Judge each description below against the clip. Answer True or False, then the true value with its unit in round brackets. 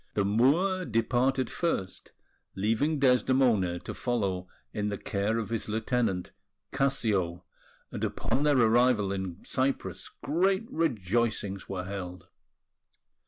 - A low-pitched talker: True (115 Hz)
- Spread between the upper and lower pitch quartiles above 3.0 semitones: True (5.1 semitones)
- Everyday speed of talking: False (115 wpm)